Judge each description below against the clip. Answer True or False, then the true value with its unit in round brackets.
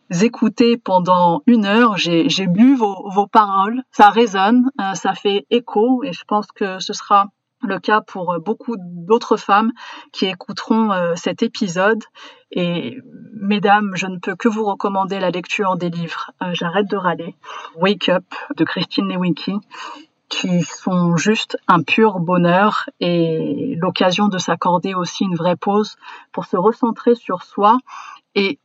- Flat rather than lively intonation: False (3.8 semitones)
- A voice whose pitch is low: False (200 Hz)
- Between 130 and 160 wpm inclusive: True (150 wpm)